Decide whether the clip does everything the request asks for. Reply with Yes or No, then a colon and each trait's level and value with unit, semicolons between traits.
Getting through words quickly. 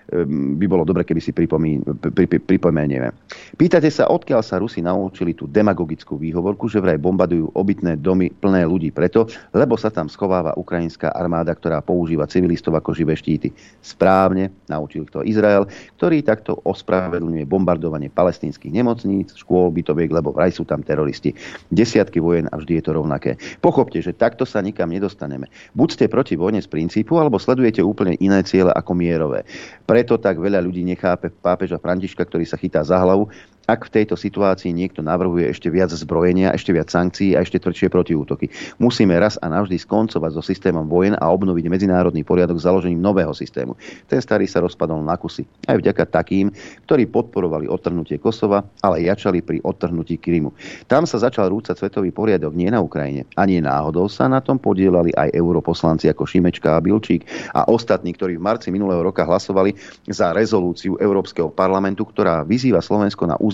Yes: fast, 170 wpm